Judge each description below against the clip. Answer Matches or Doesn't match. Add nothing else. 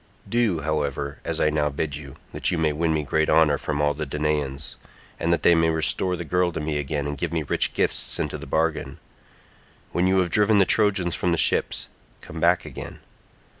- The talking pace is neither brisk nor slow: Doesn't match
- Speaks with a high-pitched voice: Doesn't match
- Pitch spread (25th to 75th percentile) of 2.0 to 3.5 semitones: Matches